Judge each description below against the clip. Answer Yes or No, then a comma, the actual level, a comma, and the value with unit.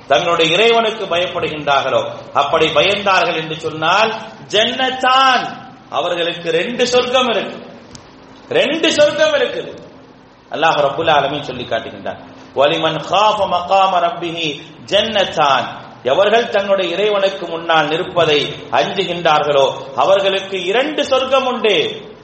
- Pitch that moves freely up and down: Yes, wide, 6.6 semitones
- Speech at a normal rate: No, slow, 90 wpm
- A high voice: Yes, high, 195 Hz